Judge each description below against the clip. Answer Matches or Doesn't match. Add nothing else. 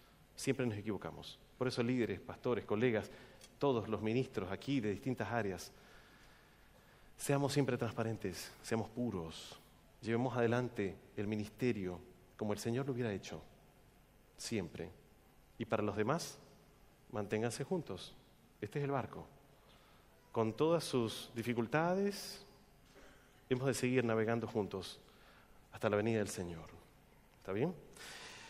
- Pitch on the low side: Matches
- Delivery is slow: Matches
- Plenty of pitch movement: Doesn't match